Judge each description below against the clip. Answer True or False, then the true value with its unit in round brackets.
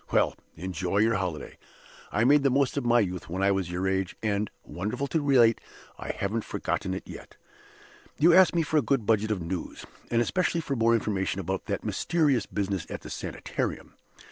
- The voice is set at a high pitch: False (110 Hz)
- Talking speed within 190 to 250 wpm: True (195 wpm)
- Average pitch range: False (6.2 semitones)